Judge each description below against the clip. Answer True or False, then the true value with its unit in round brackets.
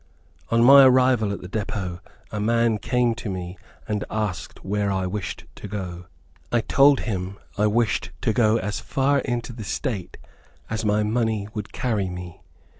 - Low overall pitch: True (105 Hz)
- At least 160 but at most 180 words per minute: True (170 wpm)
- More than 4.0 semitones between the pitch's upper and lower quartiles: False (3.4 semitones)